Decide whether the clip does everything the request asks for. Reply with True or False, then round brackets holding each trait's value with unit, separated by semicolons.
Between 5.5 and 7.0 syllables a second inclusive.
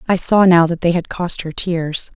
False (4.6 syllables/s)